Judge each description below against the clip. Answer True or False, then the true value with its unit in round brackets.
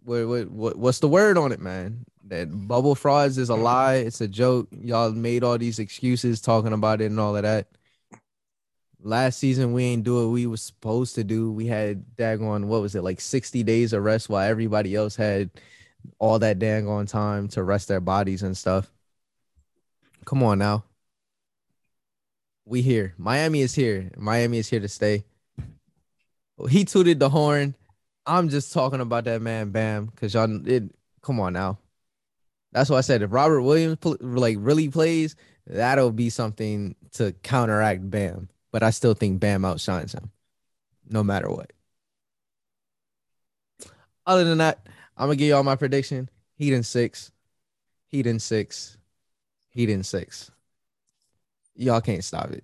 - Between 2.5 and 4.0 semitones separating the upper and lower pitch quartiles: True (3.5 semitones)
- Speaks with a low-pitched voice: True (115 Hz)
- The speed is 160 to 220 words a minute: True (165 wpm)